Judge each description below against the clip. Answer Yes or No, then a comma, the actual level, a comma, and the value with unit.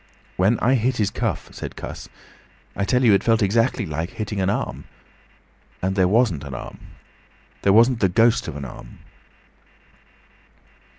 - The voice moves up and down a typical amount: Yes, average, 4.0 semitones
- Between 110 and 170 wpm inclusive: Yes, average, 160 wpm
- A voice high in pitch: No, low, 100 Hz